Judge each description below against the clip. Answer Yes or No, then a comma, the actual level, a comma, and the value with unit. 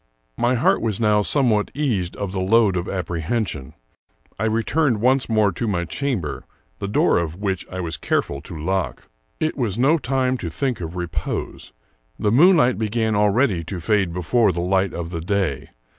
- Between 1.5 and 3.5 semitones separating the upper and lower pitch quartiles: No, average, 5.2 semitones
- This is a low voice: Yes, low, 100 Hz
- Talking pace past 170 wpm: Yes, average, 180 wpm